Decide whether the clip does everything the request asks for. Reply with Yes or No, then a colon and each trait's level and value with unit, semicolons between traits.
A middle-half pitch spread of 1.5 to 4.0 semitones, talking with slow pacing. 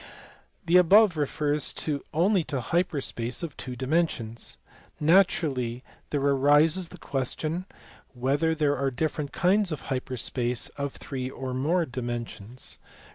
No: average, 4.4 semitones; slow, 130 wpm